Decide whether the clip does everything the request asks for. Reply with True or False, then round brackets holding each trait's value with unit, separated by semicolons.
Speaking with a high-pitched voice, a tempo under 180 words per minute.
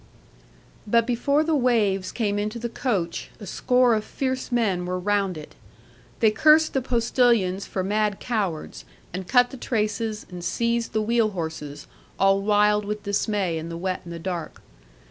True (210 Hz; 165 wpm)